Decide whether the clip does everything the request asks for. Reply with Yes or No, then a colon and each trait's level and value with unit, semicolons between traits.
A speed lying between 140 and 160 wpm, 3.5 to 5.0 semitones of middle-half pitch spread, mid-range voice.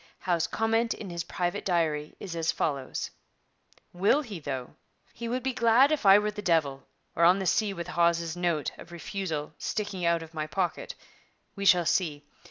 No: average, 185 wpm; average, 4.0 semitones; medium, 175 Hz